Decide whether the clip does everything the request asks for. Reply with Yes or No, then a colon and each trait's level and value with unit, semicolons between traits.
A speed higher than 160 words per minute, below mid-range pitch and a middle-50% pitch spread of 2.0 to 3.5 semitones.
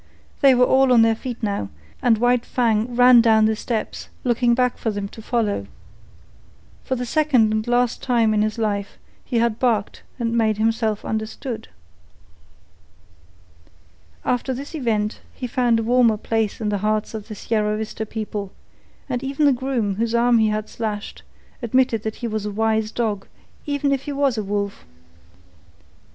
No: average, 170 wpm; high, 225 Hz; narrow, 2.4 semitones